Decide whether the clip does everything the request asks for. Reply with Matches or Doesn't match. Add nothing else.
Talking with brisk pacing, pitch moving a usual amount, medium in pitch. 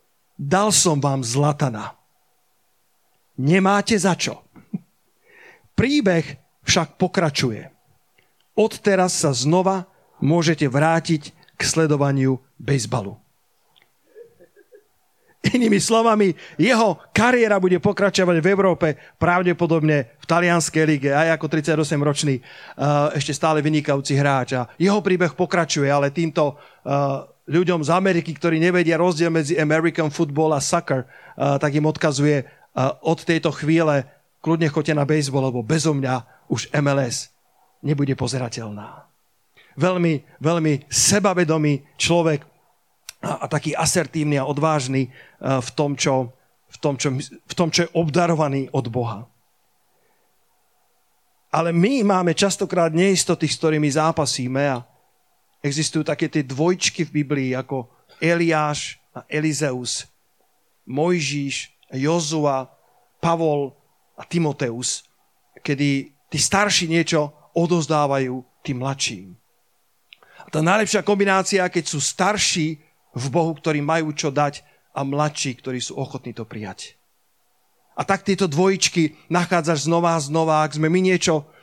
Doesn't match